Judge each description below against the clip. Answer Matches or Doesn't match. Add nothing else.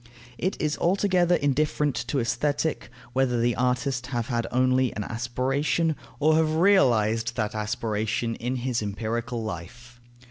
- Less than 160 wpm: Matches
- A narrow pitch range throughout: Doesn't match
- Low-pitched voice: Matches